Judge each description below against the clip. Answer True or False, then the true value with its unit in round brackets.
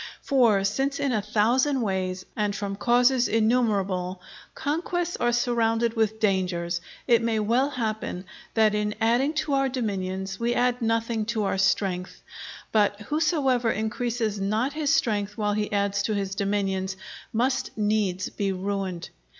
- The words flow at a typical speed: True (145 wpm)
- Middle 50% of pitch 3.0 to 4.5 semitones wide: True (3.6 semitones)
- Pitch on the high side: True (215 Hz)